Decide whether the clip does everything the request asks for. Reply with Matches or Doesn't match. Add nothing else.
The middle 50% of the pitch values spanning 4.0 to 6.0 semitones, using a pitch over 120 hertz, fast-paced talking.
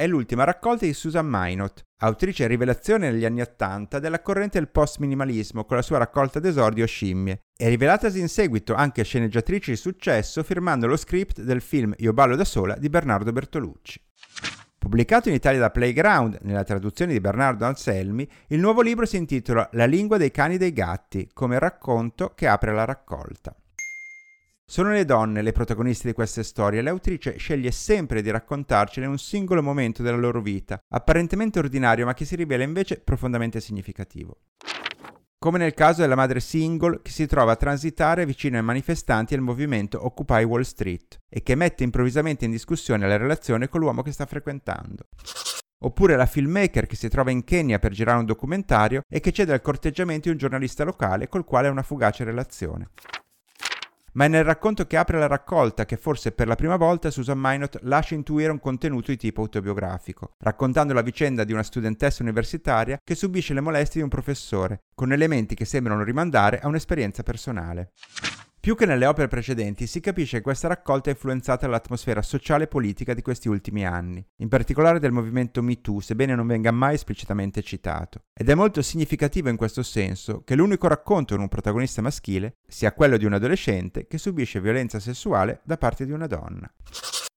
Matches